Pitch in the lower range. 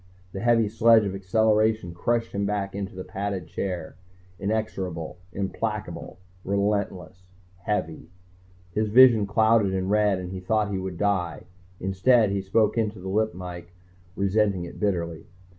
Yes: low, 100 Hz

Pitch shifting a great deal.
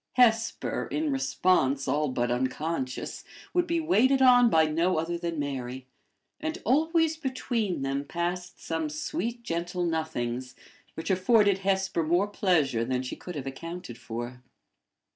Yes: wide, 8.7 semitones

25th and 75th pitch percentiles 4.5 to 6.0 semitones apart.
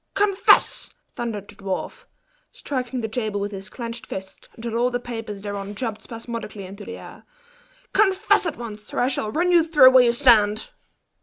No: average, 3.7 semitones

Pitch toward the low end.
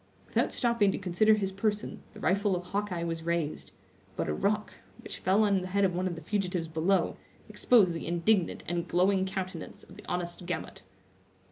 No: medium, 185 Hz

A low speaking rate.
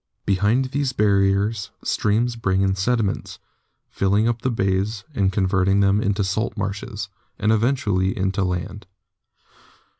Yes: slow, 125 wpm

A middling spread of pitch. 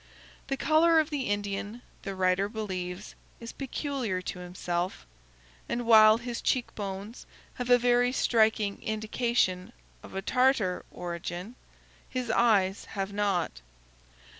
Yes: average, 4.4 semitones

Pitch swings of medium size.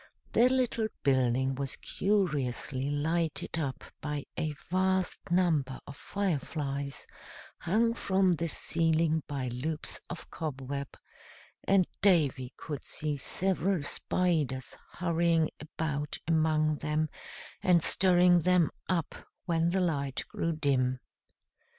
Yes: average, 4.1 semitones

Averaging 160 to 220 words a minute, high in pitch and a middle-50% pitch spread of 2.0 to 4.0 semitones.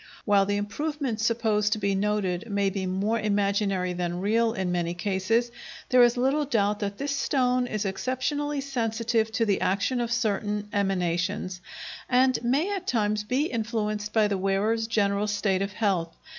Yes: average, 165 wpm; high, 210 Hz; average, 3.3 semitones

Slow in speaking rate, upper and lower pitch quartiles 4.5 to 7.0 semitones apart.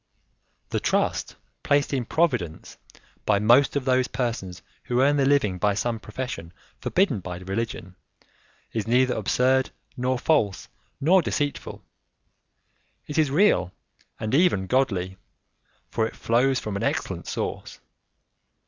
Yes: slow, 130 wpm; average, 5.2 semitones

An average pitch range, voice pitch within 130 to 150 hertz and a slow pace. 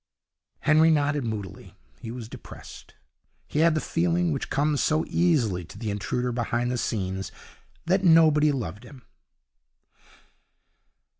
No: wide, 5.8 semitones; low, 135 Hz; slow, 130 wpm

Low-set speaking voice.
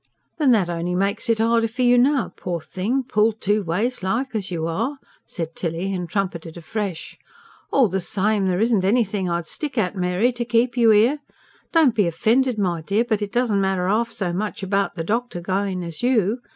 No: high, 205 Hz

